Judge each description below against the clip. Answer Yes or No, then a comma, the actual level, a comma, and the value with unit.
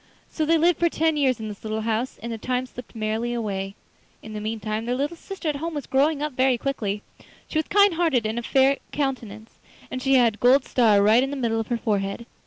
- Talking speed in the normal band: No, fast, 240 wpm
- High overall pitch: Yes, high, 245 Hz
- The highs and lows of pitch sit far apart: No, average, 4.5 semitones